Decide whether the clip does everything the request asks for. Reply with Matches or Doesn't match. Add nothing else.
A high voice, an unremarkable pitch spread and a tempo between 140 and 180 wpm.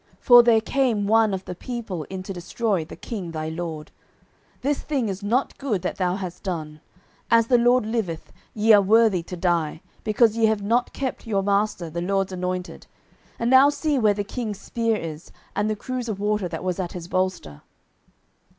Doesn't match